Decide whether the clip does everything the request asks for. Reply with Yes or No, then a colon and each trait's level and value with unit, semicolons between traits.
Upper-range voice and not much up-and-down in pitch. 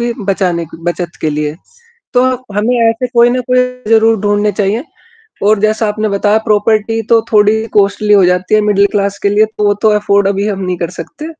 Yes: high, 210 Hz; narrow, 1.7 semitones